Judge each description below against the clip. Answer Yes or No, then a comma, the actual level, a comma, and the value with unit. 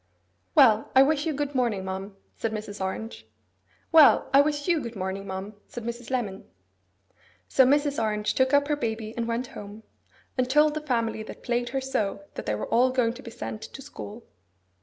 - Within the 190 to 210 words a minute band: Yes, average, 195 wpm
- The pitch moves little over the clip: No, average, 4.3 semitones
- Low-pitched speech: No, high, 235 Hz